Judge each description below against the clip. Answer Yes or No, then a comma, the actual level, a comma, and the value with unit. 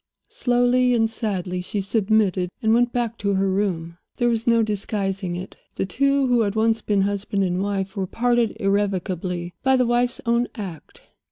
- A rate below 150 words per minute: No, average, 175 wpm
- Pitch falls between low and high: No, high, 205 Hz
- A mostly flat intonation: No, average, 3.7 semitones